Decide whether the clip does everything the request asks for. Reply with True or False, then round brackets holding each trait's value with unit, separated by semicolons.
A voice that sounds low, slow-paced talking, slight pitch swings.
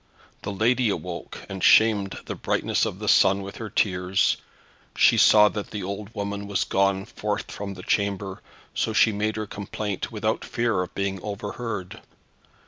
False (100 Hz; 165 wpm; 1.6 semitones)